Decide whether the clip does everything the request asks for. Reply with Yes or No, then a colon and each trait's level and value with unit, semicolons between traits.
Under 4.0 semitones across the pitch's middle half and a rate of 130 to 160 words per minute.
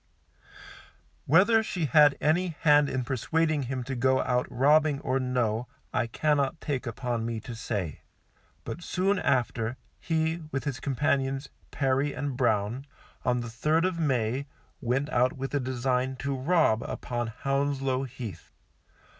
Yes: average, 3.1 semitones; average, 145 wpm